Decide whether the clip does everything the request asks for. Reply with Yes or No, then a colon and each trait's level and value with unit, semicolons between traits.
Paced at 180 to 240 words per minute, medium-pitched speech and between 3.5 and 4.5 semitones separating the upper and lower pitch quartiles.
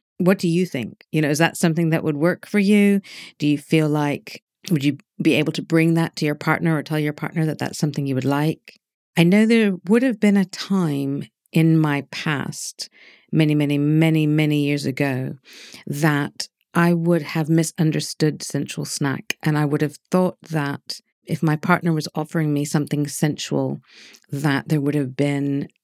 No: average, 190 wpm; medium, 155 Hz; average, 2.8 semitones